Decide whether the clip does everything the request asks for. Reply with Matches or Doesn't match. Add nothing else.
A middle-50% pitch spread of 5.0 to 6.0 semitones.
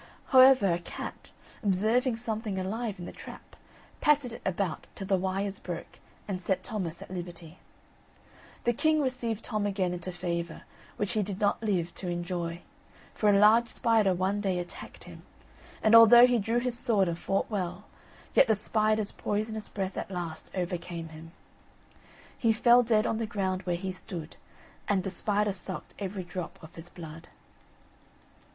Doesn't match